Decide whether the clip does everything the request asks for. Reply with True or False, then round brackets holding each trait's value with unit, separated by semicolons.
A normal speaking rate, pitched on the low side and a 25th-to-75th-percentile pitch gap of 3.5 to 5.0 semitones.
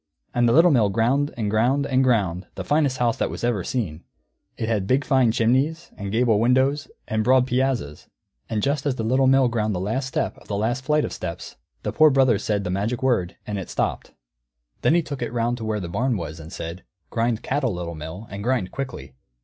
False (220 wpm; 115 Hz; 4.6 semitones)